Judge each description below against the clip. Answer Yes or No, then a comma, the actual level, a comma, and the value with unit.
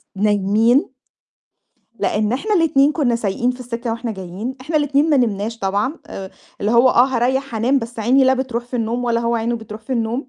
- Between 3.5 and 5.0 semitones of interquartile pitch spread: No, average, 3.0 semitones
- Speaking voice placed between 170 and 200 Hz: No, high, 235 Hz